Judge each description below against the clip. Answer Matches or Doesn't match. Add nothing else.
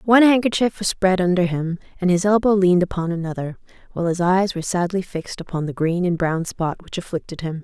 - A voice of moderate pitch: Matches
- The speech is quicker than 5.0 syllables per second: Matches